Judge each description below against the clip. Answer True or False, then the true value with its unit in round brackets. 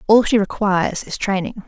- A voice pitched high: True (200 Hz)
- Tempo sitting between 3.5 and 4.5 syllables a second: False (5.3 syllables/s)